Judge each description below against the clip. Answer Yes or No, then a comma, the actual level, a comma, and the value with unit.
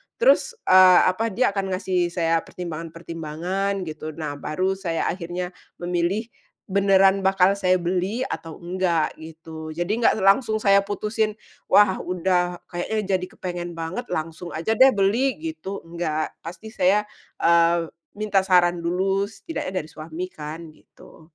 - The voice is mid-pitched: Yes, medium, 180 Hz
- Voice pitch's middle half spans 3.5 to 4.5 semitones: No, average, 2.9 semitones